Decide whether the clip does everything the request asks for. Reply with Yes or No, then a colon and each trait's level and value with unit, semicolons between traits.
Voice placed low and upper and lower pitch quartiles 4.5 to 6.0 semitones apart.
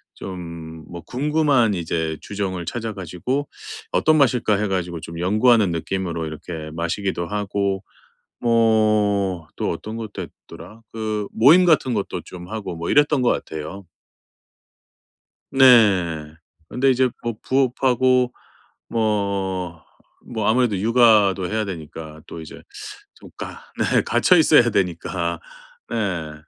Yes: low, 100 Hz; wide, 5.4 semitones